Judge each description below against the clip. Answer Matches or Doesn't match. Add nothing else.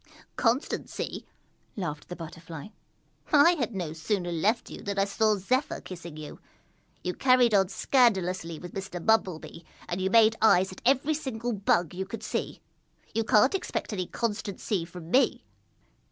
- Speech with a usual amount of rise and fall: Matches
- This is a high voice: Matches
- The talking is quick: Doesn't match